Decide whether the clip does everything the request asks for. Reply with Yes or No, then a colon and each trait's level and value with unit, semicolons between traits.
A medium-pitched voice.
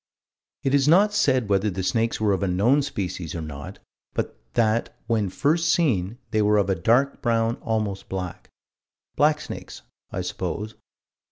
No: low, 110 Hz